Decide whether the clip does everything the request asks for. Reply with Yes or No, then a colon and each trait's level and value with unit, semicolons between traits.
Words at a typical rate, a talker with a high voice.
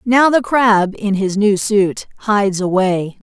Yes: average, 165 wpm; high, 205 Hz